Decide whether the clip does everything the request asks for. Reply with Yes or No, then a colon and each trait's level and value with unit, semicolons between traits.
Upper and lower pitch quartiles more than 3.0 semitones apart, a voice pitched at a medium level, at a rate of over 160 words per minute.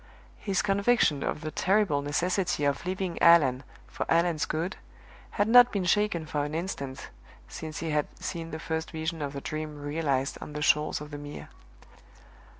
Yes: average, 3.7 semitones; medium, 160 Hz; average, 170 wpm